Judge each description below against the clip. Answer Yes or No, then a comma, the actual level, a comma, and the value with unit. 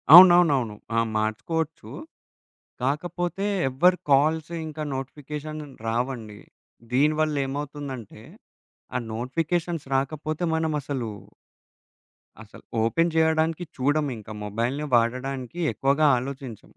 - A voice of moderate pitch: Yes, medium, 145 Hz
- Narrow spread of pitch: No, average, 3.9 semitones